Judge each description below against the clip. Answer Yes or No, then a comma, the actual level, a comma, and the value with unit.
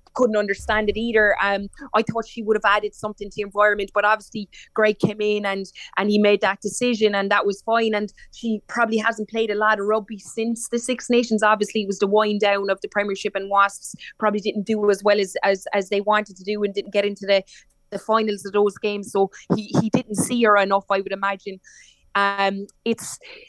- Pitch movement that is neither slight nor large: No, narrow, 1.5 semitones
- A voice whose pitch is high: Yes, high, 210 Hz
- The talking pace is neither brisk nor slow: No, fast, 225 wpm